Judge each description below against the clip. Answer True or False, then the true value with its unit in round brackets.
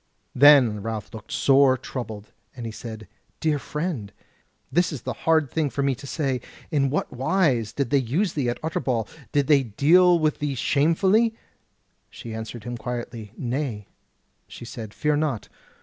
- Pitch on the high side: False (135 Hz)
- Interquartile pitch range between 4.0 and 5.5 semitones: True (4.6 semitones)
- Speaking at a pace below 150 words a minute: False (165 wpm)